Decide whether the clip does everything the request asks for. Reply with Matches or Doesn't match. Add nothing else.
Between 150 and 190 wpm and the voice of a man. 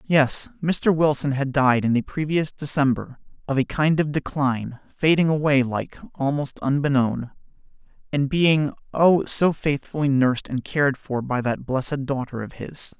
Matches